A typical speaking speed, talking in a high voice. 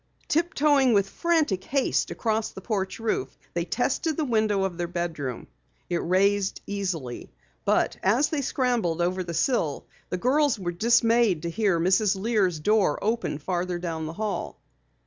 Yes: average, 155 wpm; high, 200 Hz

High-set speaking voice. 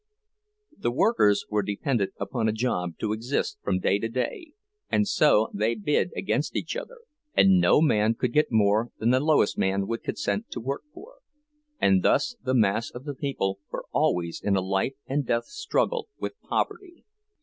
No: low, 115 Hz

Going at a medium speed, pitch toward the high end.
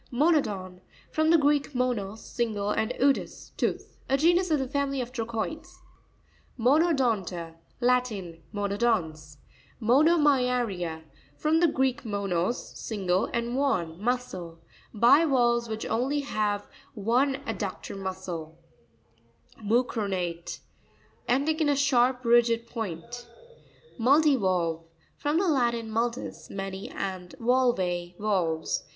No: slow, 105 wpm; high, 235 Hz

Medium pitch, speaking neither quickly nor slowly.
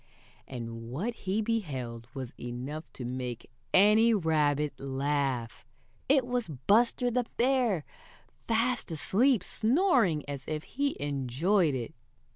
No: medium, 155 Hz; slow, 115 wpm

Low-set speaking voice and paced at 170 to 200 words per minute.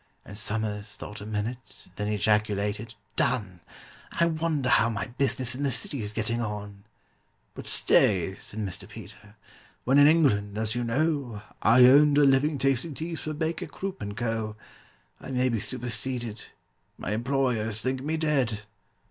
No: low, 120 Hz; average, 150 wpm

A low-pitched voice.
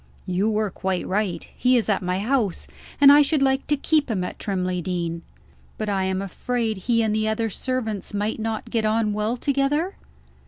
No: high, 215 Hz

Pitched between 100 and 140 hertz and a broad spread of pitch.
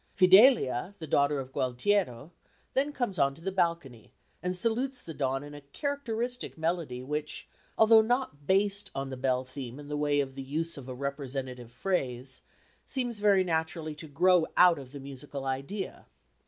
No: medium, 150 Hz; wide, 6.3 semitones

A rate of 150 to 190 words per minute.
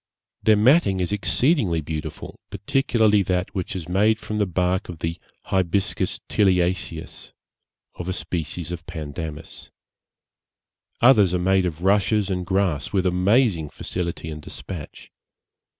No: slow, 135 wpm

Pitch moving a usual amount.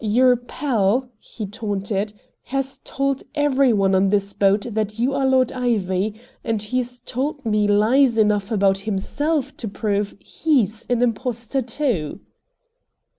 Yes: average, 4.1 semitones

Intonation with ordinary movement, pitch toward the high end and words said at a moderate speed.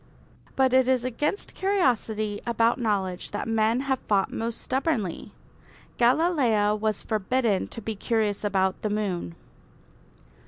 No: average, 3.7 semitones; high, 225 Hz; slow, 125 wpm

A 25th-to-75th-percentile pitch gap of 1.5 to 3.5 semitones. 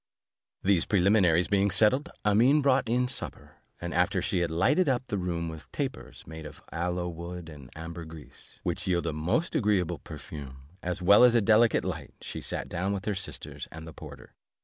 No: average, 4.5 semitones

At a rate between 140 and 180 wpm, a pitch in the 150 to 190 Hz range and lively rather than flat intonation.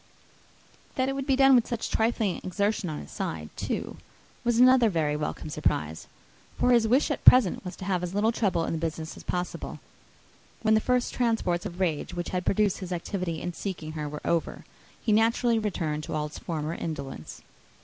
No: average, 200 wpm; medium, 185 Hz; wide, 6.0 semitones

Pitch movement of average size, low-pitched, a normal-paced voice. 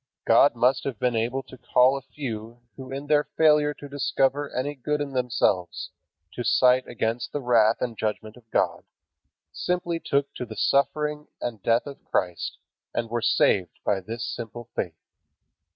Yes: average, 3.7 semitones; low, 125 Hz; average, 170 wpm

